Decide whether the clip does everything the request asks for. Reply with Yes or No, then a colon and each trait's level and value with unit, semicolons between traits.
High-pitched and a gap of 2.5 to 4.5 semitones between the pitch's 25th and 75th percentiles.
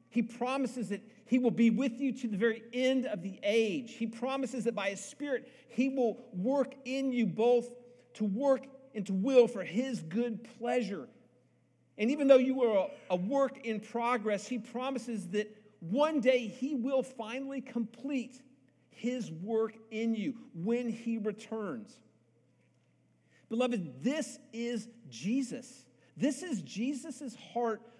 Yes: high, 235 Hz; average, 2.9 semitones